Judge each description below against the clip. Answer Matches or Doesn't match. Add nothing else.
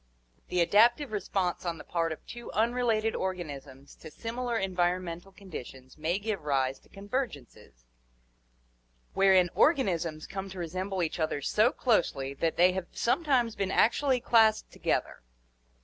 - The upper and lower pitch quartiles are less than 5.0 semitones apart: Doesn't match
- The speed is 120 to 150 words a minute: Matches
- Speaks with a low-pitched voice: Doesn't match